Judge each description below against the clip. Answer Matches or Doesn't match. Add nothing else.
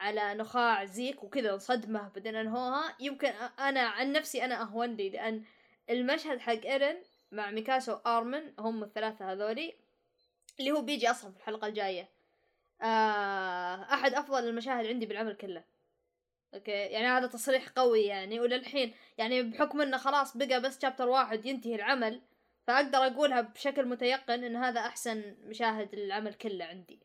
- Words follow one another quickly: Matches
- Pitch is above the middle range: Matches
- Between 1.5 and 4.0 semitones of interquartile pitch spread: Matches